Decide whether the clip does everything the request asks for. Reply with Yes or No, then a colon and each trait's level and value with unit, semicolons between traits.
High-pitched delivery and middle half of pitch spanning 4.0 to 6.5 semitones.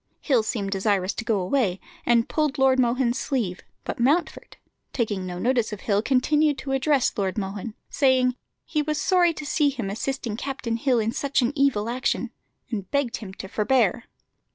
Yes: high, 245 Hz; average, 4.6 semitones